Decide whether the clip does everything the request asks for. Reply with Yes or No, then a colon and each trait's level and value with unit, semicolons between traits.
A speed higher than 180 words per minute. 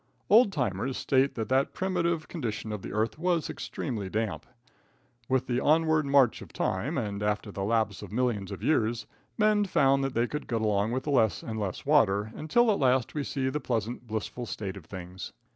Yes: average, 195 wpm